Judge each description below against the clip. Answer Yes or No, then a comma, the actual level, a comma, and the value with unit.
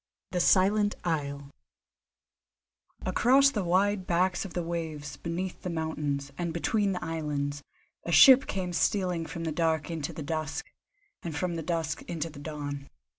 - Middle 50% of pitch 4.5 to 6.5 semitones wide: No, average, 3.3 semitones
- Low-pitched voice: No, medium, 165 Hz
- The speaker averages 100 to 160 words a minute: Yes, average, 155 wpm